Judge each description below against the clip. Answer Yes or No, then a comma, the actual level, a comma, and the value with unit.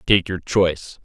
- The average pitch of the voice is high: No, very low, 90 Hz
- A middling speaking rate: Yes, average, 175 wpm